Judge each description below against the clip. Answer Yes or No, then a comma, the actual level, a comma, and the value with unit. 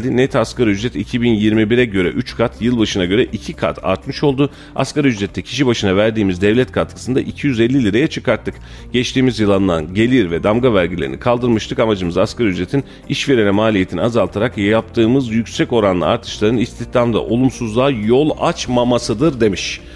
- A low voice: Yes, low, 115 Hz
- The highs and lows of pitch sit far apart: No, average, 4.0 semitones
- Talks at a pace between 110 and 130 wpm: No, fast, 140 wpm